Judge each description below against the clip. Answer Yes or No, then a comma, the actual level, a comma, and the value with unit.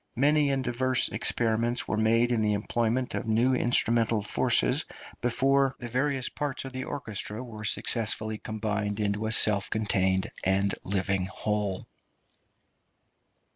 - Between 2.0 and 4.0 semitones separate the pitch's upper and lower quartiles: Yes, average, 3.2 semitones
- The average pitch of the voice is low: Yes, low, 110 Hz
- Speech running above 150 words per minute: No, slow, 135 wpm